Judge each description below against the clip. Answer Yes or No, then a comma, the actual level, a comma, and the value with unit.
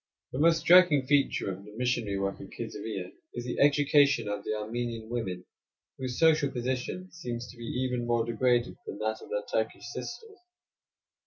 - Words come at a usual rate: Yes, average, 170 wpm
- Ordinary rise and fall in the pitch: Yes, average, 4.4 semitones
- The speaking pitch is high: No, low, 120 Hz